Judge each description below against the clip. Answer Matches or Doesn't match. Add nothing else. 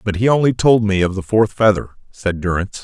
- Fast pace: Matches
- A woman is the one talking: Doesn't match